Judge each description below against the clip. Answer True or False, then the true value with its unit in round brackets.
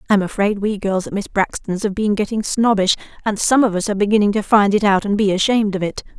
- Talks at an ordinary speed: False (250 wpm)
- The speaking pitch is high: True (205 Hz)